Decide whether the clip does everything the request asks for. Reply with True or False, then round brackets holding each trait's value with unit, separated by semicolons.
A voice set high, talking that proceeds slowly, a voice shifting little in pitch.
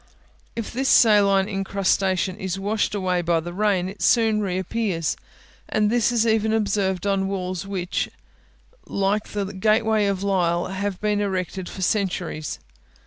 False (195 Hz; 145 wpm; 2.2 semitones)